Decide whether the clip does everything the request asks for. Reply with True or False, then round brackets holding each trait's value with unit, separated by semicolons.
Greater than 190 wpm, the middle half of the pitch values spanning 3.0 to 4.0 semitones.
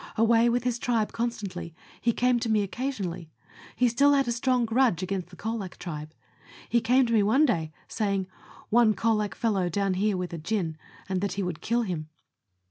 False (200 wpm; 4.4 semitones)